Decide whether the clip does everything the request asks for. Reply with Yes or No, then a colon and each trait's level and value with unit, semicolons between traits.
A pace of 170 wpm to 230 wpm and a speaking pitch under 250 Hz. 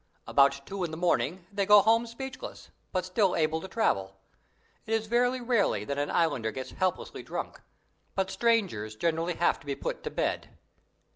Yes: average, 175 wpm; medium, 185 Hz